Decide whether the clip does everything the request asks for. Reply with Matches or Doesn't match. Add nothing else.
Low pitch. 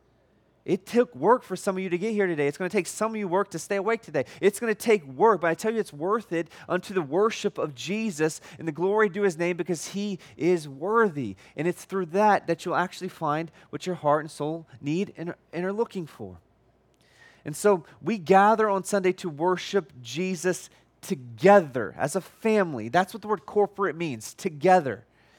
Doesn't match